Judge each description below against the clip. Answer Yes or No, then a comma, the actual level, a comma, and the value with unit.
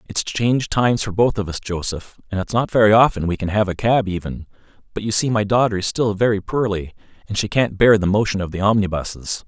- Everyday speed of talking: No, fast, 235 wpm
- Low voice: Yes, low, 105 Hz